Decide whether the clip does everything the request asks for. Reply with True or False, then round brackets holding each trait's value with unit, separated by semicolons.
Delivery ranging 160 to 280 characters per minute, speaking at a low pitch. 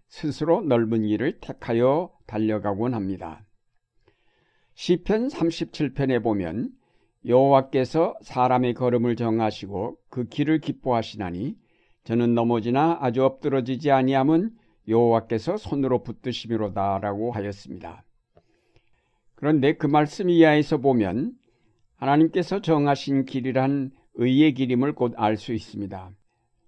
True (270 characters per minute; 125 Hz)